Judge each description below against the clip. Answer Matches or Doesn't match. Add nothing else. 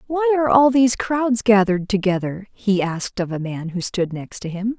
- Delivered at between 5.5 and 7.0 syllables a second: Doesn't match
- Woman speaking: Matches